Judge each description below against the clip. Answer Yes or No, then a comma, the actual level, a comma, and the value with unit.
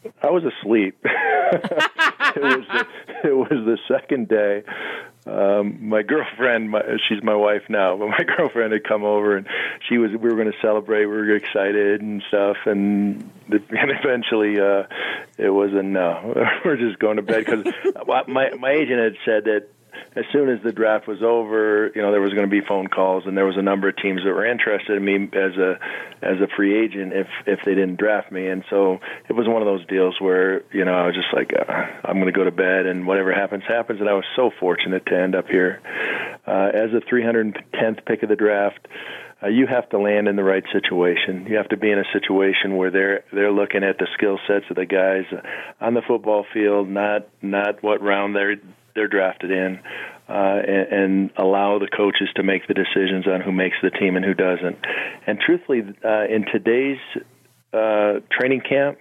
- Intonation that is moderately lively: No, narrow, 2.0 semitones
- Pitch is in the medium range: No, low, 100 Hz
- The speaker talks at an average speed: No, fast, 210 wpm